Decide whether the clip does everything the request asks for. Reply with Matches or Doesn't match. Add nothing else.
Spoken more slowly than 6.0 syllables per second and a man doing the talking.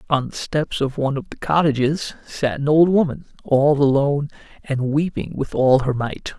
Matches